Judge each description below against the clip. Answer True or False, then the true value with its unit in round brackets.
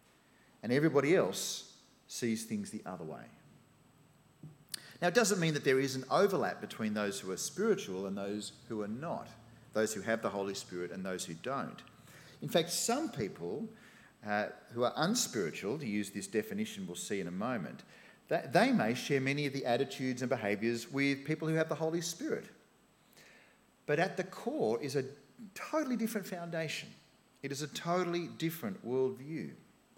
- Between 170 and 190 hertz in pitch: False (140 Hz)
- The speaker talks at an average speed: True (170 wpm)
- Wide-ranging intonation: True (6.7 semitones)